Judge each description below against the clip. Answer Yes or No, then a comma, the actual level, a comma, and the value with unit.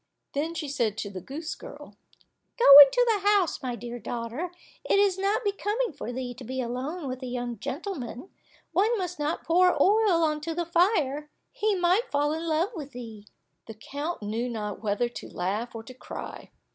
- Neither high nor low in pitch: No, very high, 295 Hz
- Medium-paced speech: Yes, average, 190 wpm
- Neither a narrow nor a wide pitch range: No, wide, 7.0 semitones